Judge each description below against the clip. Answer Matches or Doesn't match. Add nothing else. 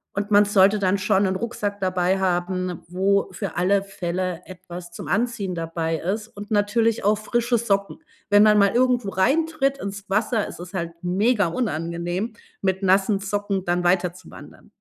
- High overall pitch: Matches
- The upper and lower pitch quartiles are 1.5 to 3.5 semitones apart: Matches